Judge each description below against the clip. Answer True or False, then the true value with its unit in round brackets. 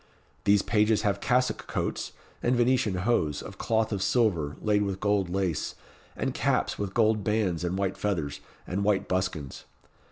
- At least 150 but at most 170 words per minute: True (160 wpm)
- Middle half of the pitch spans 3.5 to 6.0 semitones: False (2.9 semitones)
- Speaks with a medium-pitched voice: False (100 Hz)